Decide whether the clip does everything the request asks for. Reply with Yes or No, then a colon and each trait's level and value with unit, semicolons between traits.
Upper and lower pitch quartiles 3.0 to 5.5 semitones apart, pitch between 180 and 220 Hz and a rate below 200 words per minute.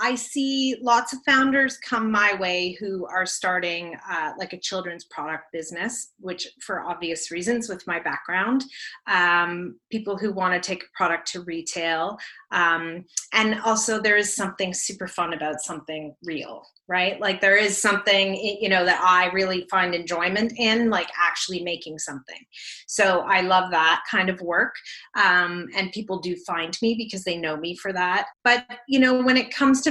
Yes: average, 3.9 semitones; medium, 185 Hz; average, 175 wpm